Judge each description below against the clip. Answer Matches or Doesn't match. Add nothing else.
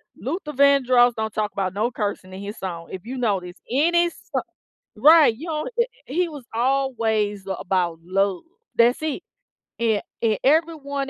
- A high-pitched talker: Matches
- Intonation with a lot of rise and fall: Matches